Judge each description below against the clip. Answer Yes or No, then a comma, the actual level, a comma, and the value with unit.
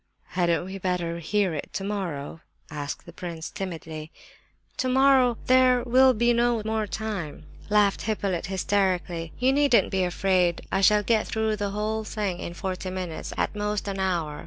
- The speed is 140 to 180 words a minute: Yes, average, 160 wpm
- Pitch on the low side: No, high, 195 Hz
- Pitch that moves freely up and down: No, average, 4.0 semitones